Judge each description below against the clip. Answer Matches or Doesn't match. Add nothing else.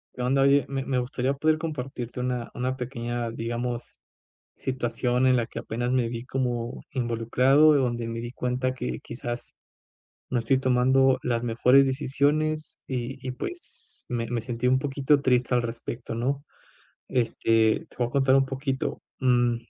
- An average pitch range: Doesn't match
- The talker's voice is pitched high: Doesn't match